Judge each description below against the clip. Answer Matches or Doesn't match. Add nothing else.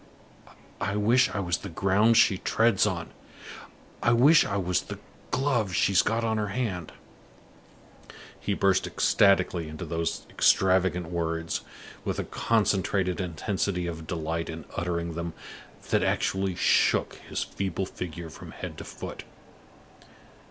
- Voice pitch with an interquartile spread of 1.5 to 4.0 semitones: Matches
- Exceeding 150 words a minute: Doesn't match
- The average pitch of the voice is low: Matches